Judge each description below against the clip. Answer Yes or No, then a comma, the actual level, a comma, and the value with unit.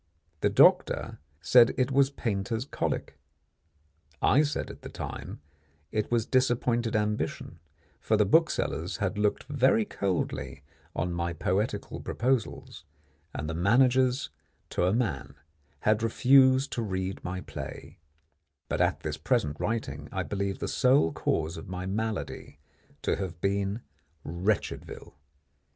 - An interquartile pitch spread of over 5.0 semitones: Yes, wide, 5.4 semitones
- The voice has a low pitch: Yes, low, 105 Hz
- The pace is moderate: No, slow, 130 wpm